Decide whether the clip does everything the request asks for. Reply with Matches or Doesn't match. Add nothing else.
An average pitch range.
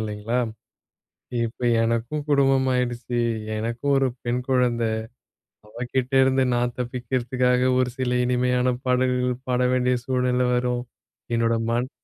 Doesn't match